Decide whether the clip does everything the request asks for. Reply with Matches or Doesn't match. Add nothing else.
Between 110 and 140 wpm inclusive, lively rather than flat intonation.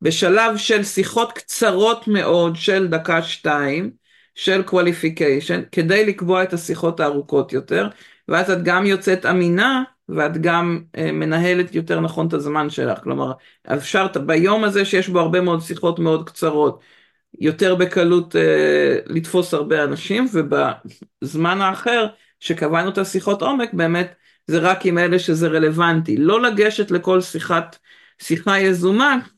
Doesn't match